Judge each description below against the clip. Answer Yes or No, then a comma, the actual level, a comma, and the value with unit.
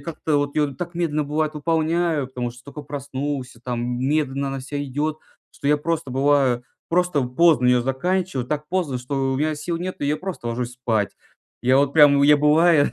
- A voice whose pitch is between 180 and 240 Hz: No, medium, 145 Hz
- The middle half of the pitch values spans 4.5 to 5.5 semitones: No, average, 3.1 semitones